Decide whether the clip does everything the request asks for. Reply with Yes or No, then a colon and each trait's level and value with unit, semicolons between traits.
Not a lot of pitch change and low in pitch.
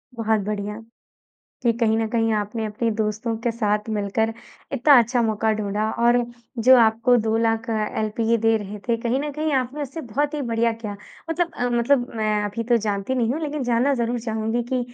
No: narrow, 2.2 semitones; high, 230 Hz